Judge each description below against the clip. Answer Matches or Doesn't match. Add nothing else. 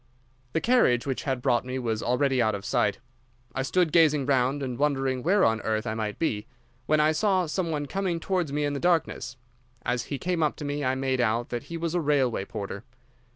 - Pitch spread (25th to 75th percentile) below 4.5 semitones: Doesn't match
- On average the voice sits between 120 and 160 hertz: Matches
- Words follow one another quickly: Matches